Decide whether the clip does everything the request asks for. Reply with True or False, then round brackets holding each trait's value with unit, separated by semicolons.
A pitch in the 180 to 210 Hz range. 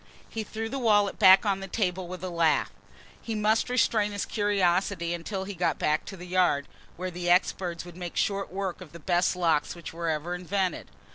True (185 Hz)